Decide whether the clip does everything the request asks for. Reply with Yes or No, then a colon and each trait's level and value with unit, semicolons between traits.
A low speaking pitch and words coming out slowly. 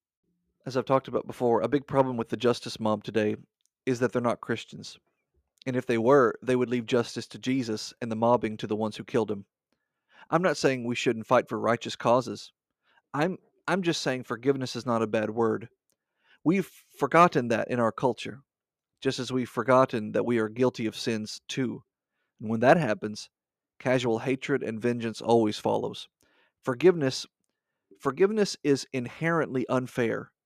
No: low, 125 Hz; average, 175 wpm